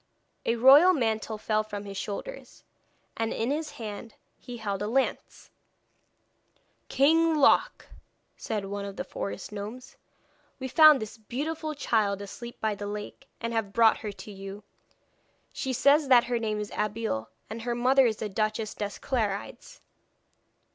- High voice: Yes, high, 225 Hz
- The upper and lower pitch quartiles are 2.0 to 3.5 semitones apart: No, average, 4.0 semitones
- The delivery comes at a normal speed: Yes, average, 155 wpm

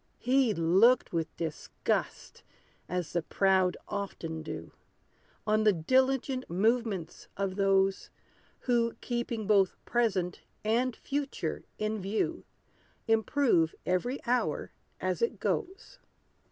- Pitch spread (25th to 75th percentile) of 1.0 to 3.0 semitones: No, average, 5.0 semitones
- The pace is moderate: No, slow, 105 wpm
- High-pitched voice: Yes, high, 215 Hz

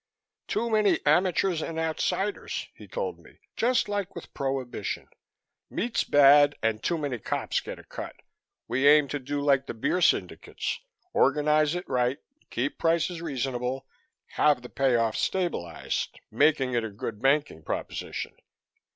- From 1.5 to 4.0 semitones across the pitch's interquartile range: No, average, 5.1 semitones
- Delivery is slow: No, average, 145 wpm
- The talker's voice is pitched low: No, medium, 145 Hz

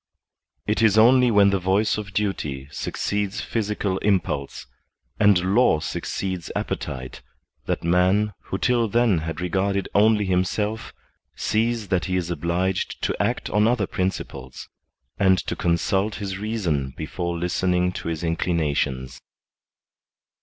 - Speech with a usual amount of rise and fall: Yes, average, 3.6 semitones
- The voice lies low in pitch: Yes, very low, 95 Hz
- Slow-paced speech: Yes, slow, 130 wpm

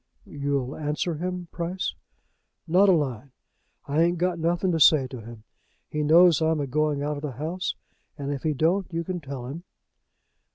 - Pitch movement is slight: No, average, 3.5 semitones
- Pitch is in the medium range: Yes, medium, 155 Hz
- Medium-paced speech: Yes, average, 180 wpm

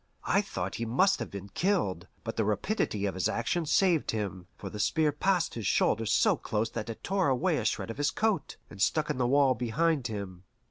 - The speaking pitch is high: No, low, 120 Hz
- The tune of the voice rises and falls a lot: Yes, wide, 7.3 semitones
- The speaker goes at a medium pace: No, fast, 220 wpm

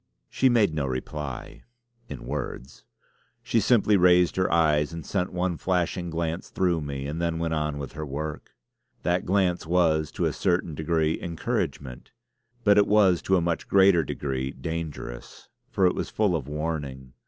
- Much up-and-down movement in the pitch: No, average, 3.3 semitones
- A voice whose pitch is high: No, very low, 85 Hz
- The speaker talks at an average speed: Yes, average, 165 wpm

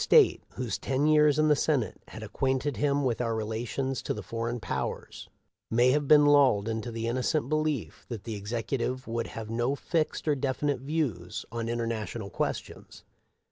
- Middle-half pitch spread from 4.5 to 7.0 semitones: No, average, 4.1 semitones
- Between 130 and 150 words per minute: No, average, 180 wpm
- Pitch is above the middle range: No, low, 125 Hz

